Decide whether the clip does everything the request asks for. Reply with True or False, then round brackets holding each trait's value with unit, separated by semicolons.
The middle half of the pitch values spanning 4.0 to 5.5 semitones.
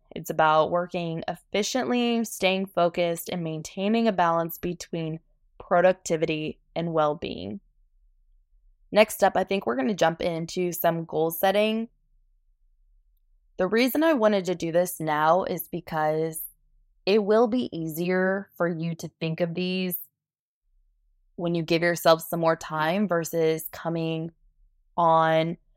False (2.5 semitones)